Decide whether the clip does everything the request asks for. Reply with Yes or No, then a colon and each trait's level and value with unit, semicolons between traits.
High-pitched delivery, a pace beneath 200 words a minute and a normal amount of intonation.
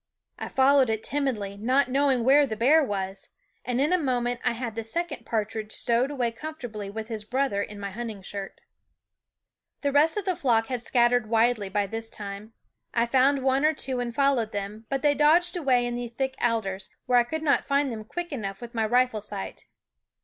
No: high, 240 Hz; fast, 205 wpm; average, 4.1 semitones